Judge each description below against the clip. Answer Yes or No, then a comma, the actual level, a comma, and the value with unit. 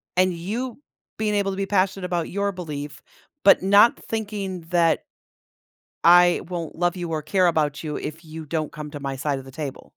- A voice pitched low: No, medium, 175 Hz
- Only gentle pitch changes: No, average, 4.1 semitones